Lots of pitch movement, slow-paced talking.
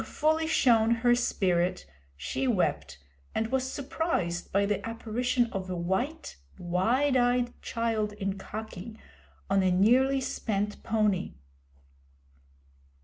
No: average, 4.5 semitones; slow, 120 wpm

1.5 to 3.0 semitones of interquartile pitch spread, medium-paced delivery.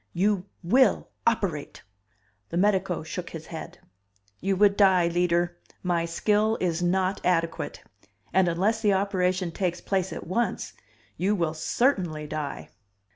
No: average, 2.7 semitones; slow, 130 wpm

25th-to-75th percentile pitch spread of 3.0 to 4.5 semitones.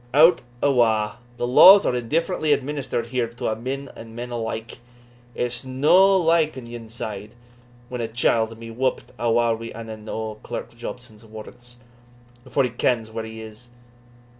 No: narrow, 2.6 semitones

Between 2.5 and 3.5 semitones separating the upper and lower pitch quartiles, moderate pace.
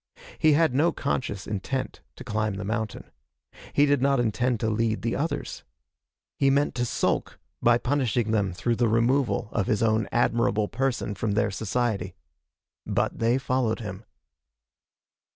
Yes: average, 3.2 semitones; average, 150 wpm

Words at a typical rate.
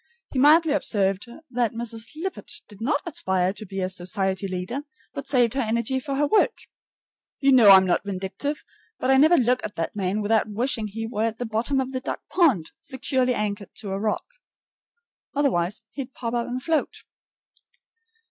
Yes: average, 180 wpm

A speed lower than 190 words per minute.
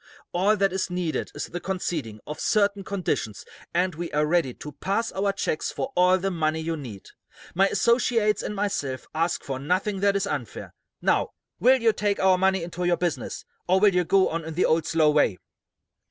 No: average, 195 wpm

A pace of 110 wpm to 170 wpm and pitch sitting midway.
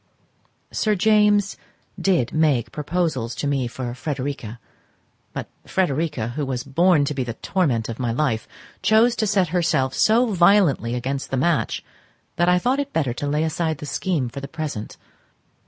Yes: average, 165 wpm; medium, 150 Hz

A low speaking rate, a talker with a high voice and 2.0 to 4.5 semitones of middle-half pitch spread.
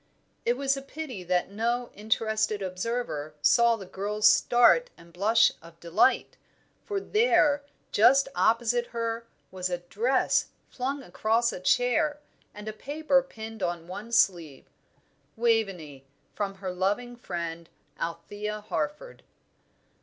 No: slow, 125 wpm; high, 220 Hz; average, 5.0 semitones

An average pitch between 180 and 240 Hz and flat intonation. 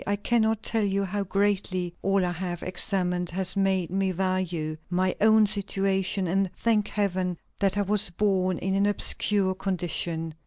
Yes: high, 190 Hz; narrow, 1.9 semitones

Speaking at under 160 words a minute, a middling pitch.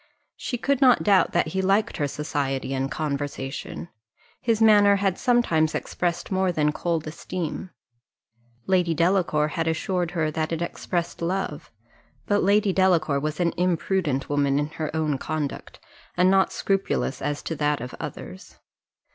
Yes: average, 150 wpm; medium, 170 Hz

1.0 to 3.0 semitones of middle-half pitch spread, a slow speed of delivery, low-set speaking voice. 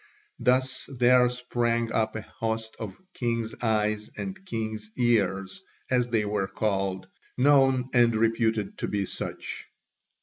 Yes: narrow, 2.6 semitones; slow, 130 wpm; low, 115 Hz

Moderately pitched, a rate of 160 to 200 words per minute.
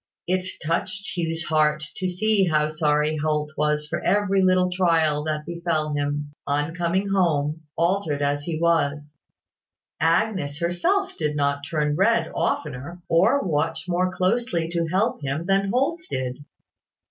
No: medium, 165 Hz; average, 145 wpm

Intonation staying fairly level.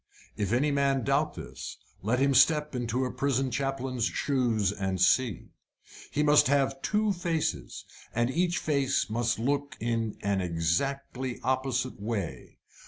No: average, 3.7 semitones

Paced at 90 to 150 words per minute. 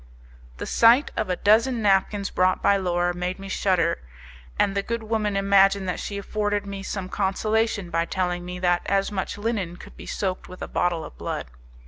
No: average, 190 wpm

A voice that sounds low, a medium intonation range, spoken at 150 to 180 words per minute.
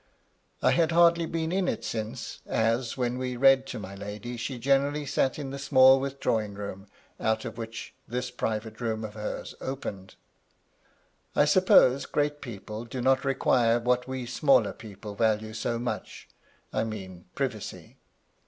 Yes: low, 120 Hz; average, 3.6 semitones; average, 160 wpm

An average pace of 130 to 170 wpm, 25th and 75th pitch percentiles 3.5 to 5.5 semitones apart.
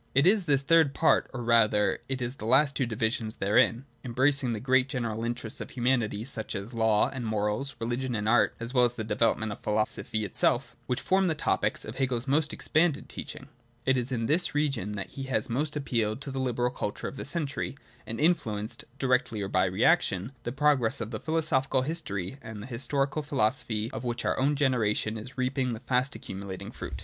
No: average, 200 wpm; average, 3.9 semitones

